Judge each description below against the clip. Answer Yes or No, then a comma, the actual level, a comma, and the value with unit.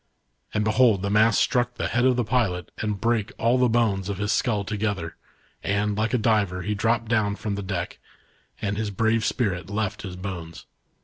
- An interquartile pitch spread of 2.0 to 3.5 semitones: Yes, narrow, 2.4 semitones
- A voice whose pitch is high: No, low, 105 Hz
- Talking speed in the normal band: Yes, average, 195 wpm